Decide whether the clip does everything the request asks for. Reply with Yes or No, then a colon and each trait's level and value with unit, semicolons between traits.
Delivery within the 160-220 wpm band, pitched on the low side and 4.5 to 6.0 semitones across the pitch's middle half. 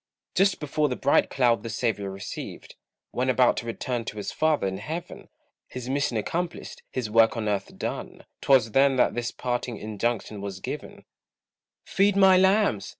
Yes: average, 165 wpm; low, 125 Hz; average, 5.0 semitones